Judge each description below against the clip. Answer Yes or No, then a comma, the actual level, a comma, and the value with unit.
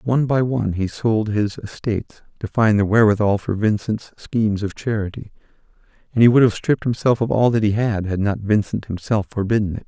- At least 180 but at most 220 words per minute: Yes, average, 200 wpm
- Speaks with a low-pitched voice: Yes, low, 110 Hz